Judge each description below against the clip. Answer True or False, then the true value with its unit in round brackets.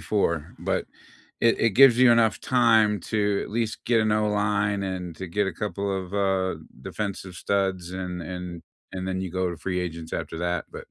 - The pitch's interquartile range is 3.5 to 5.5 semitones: False (2.9 semitones)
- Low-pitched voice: True (95 Hz)